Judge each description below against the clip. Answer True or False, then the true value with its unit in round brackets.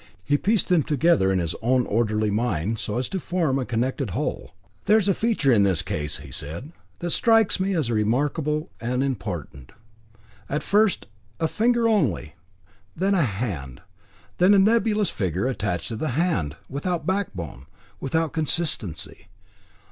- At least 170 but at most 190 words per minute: False (155 wpm)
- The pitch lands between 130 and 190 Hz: True (135 Hz)